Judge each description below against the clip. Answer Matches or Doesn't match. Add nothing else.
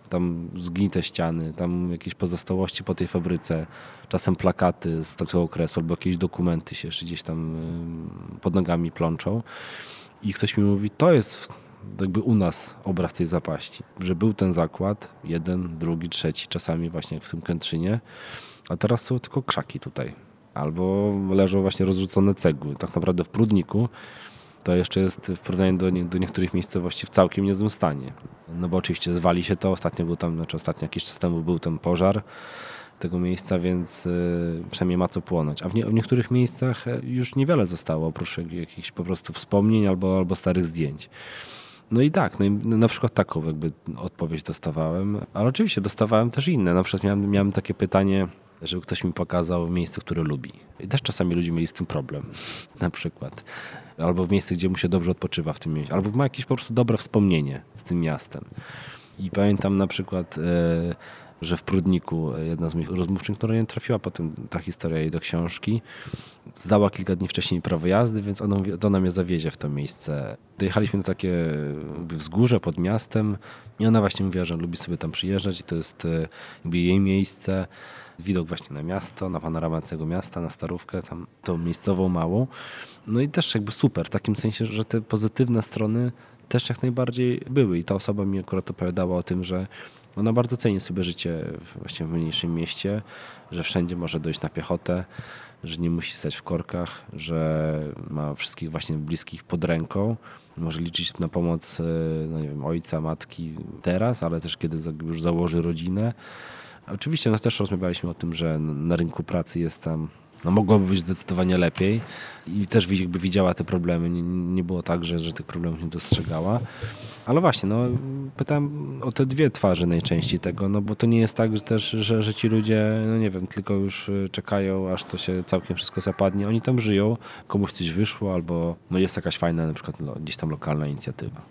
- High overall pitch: Doesn't match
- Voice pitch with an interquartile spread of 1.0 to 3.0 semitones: Doesn't match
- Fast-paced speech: Matches